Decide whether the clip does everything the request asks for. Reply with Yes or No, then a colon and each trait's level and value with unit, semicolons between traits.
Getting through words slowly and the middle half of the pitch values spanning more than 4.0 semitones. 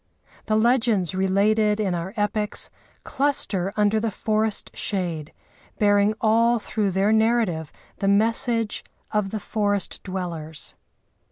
No: slow, 115 wpm; narrow, 2.4 semitones